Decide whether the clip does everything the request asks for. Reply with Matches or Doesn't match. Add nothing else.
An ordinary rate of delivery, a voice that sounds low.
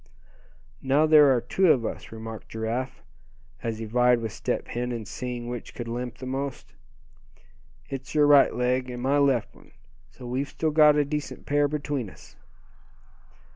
Matches